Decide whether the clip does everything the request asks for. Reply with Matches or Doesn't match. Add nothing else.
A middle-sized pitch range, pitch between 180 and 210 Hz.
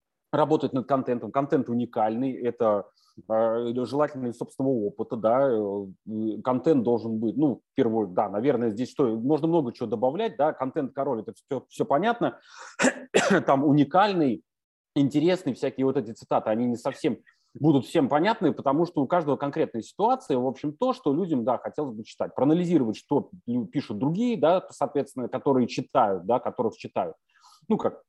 Doesn't match